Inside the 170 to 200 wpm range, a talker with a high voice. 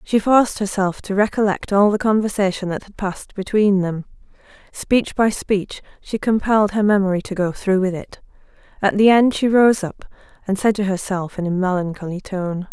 Yes: average, 185 wpm; high, 200 Hz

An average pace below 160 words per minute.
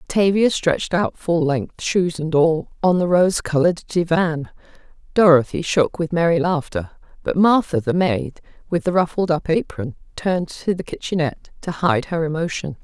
No: average, 165 wpm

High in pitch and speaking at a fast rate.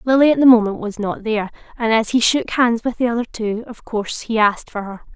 Yes: high, 225 Hz; fast, 255 wpm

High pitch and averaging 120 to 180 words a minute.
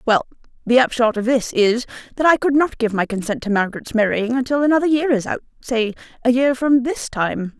No: high, 240 Hz; fast, 205 wpm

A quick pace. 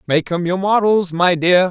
Yes: fast, 210 wpm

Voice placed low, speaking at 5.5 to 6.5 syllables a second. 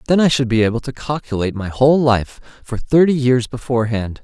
Yes: low, 125 Hz; 6.0 syllables/s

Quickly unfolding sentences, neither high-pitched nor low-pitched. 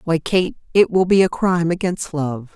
Yes: fast, 210 wpm; medium, 175 Hz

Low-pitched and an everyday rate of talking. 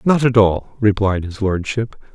Yes: low, 110 Hz; average, 170 wpm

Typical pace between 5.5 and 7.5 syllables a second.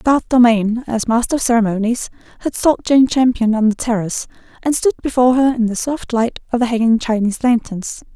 Yes: 5.6 syllables/s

